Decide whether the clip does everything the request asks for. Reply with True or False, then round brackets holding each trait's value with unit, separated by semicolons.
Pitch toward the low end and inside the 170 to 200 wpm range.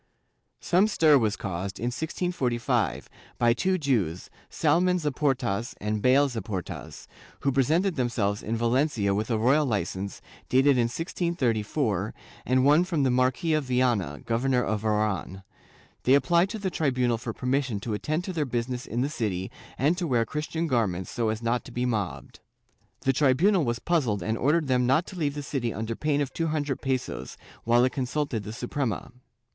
True (125 Hz; 175 wpm)